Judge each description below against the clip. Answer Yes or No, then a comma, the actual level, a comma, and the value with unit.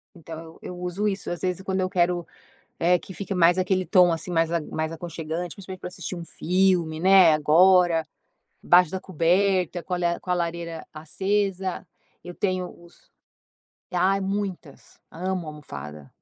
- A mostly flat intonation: Yes, narrow, 2.2 semitones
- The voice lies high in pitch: No, medium, 180 Hz